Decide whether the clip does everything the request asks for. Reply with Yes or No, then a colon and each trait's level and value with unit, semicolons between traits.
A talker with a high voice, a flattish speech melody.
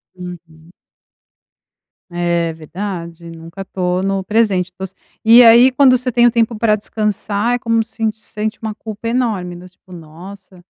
No: high, 200 Hz; average, 4.3 semitones